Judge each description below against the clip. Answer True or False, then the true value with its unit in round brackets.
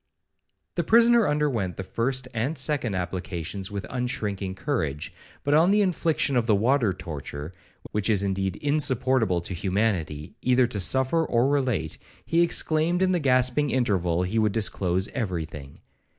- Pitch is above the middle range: False (115 Hz)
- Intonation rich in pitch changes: True (7.1 semitones)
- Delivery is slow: False (150 wpm)